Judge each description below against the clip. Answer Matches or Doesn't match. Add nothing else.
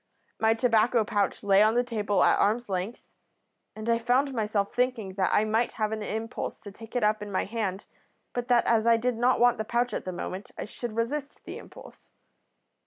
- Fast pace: Matches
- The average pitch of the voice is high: Matches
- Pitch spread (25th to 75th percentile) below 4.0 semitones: Matches